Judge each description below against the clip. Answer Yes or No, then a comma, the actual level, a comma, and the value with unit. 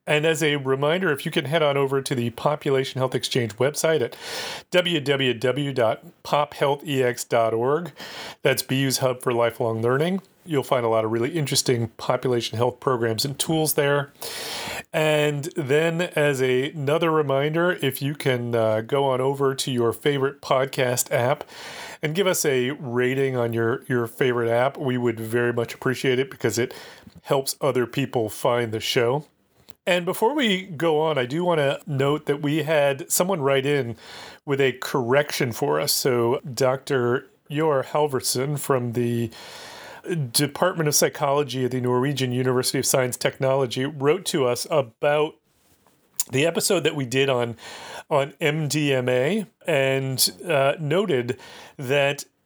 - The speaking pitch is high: No, low, 135 Hz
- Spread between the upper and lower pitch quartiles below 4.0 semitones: Yes, average, 3.0 semitones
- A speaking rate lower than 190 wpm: Yes, average, 150 wpm